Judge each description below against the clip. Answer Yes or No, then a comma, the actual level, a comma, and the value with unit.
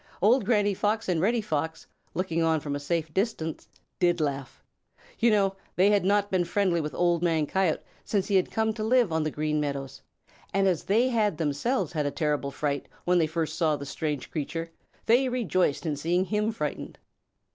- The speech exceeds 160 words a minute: Yes, average, 190 wpm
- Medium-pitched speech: Yes, medium, 175 Hz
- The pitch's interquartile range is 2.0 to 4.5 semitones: No, average, 5.1 semitones